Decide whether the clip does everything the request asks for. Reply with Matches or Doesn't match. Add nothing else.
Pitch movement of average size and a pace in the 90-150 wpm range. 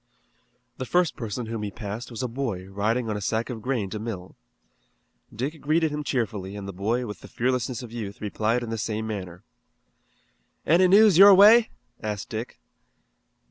Doesn't match